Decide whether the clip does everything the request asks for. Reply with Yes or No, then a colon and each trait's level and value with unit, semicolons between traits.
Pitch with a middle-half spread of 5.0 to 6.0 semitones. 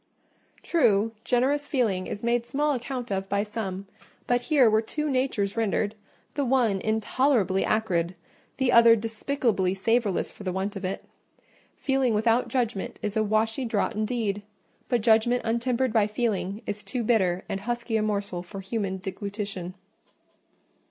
No: average, 3.5 semitones